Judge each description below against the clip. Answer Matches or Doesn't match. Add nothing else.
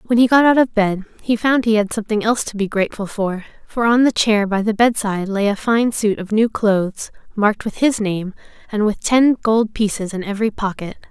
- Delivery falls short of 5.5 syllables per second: Doesn't match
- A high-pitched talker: Matches